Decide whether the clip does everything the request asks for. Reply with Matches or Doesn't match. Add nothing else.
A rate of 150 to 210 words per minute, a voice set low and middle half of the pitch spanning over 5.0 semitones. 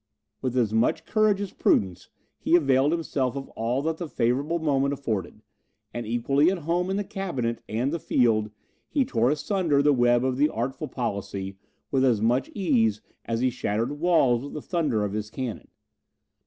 Matches